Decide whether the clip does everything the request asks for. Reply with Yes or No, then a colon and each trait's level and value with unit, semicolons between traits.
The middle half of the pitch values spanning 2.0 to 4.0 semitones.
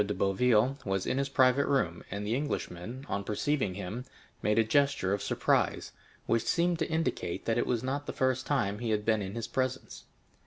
No: average, 5.1 semitones